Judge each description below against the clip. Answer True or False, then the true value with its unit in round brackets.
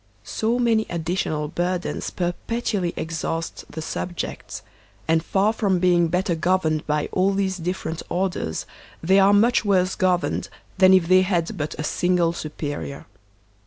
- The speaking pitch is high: False (180 Hz)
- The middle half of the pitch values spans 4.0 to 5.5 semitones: False (2.7 semitones)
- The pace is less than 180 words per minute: True (145 wpm)